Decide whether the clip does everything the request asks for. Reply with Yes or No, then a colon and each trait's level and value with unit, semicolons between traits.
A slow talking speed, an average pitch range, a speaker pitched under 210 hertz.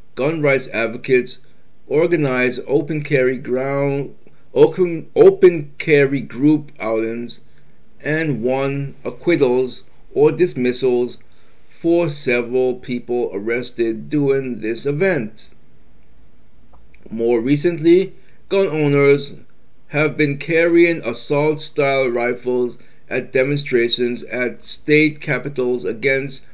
Yes: slow, 90 wpm; average, 3.6 semitones; low, 135 Hz